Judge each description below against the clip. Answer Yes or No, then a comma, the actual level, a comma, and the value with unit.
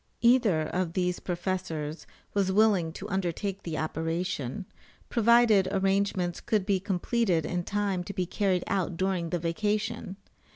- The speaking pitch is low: No, medium, 185 Hz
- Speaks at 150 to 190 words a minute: No, slow, 135 wpm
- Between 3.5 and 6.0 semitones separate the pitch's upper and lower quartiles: No, average, 2.8 semitones